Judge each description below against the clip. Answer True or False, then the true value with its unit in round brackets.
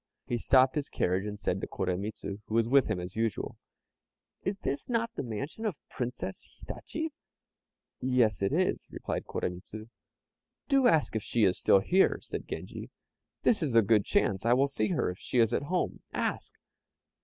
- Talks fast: False (180 wpm)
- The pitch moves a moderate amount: False (5.7 semitones)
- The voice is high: False (115 Hz)